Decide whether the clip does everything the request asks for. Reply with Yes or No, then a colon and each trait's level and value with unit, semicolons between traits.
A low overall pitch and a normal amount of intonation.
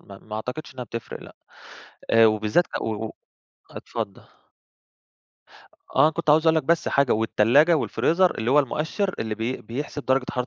No: low, 130 Hz; wide, 5.8 semitones